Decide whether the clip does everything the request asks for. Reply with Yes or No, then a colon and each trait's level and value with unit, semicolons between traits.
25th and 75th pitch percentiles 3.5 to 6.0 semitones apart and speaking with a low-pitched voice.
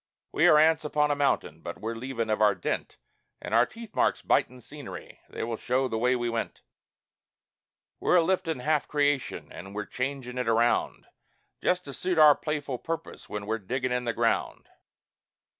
Yes: average, 4.5 semitones; low, 130 Hz